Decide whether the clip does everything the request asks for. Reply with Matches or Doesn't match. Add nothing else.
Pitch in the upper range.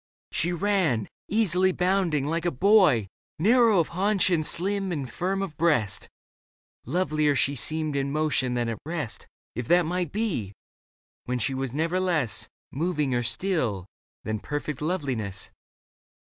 Doesn't match